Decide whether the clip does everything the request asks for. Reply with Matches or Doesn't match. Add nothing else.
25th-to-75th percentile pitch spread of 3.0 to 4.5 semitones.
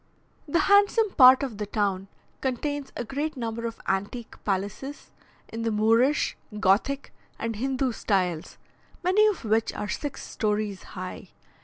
Doesn't match